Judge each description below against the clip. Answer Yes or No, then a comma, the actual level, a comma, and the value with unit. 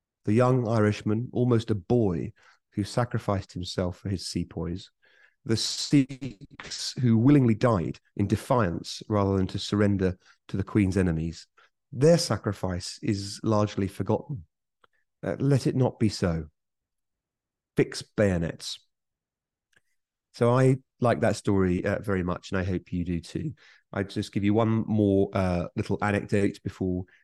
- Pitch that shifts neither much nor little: Yes, average, 3.8 semitones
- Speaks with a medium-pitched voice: No, low, 105 Hz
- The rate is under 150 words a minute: Yes, average, 140 wpm